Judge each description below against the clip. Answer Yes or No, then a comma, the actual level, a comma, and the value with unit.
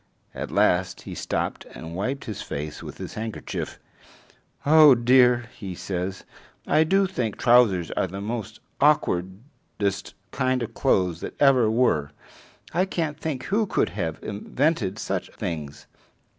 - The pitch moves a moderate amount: No, wide, 6.6 semitones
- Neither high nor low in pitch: No, low, 115 Hz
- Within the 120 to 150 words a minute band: Yes, average, 140 wpm